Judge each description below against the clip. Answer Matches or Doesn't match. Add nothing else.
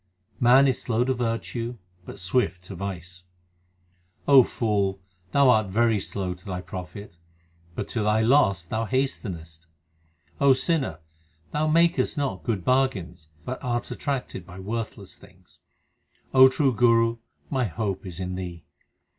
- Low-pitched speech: Matches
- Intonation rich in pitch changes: Matches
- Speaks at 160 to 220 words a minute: Doesn't match